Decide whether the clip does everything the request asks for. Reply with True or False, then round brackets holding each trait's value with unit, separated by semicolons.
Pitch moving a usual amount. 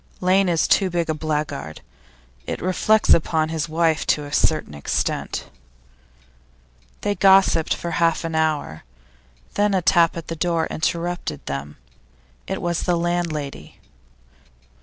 False (2.2 semitones)